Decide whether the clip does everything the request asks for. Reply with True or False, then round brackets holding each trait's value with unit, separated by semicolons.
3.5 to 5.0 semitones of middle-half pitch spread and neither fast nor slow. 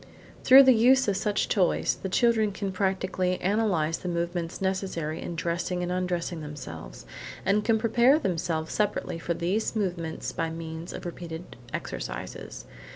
True (3.9 semitones; 150 wpm)